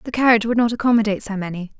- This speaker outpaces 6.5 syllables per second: Yes, 8.6 syllables/s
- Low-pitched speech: No, high, 220 Hz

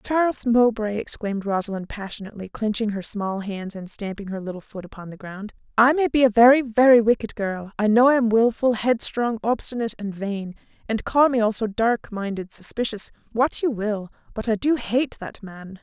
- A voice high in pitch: Yes, high, 220 Hz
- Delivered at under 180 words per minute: No, average, 185 wpm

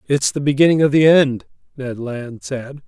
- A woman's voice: No, male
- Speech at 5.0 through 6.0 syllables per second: No, 4.7 syllables/s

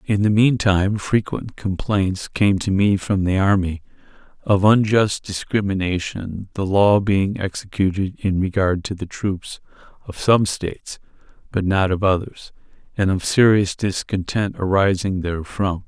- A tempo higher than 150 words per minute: No, average, 140 wpm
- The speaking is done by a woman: No, male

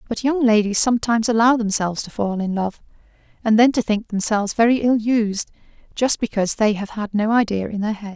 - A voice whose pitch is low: No, high, 220 Hz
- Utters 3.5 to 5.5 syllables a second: No, 5.9 syllables/s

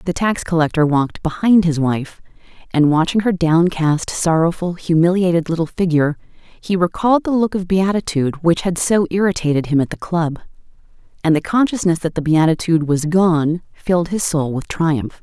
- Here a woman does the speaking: Yes, female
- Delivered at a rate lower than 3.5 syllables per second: No, 5.2 syllables/s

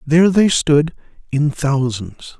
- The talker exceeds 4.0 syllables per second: No, 3.8 syllables/s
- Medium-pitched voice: Yes, medium, 150 Hz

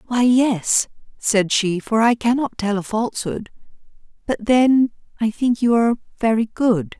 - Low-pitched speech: No, high, 225 Hz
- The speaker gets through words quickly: No, average, 155 wpm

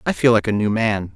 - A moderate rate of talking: No, fast, 315 wpm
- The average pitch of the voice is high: No, low, 100 Hz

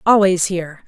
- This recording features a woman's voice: Yes, female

